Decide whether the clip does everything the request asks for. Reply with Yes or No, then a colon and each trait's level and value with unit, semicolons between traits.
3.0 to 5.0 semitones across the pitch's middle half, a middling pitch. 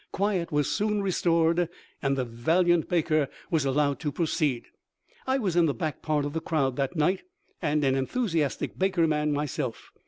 Yes: average, 3.4 semitones; medium, 155 Hz